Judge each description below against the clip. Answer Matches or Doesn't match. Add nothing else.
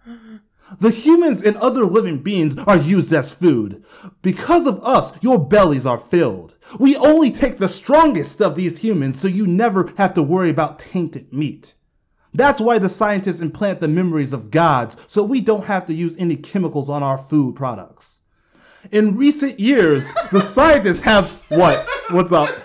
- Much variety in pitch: Matches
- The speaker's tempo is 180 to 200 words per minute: Doesn't match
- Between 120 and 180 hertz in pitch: Doesn't match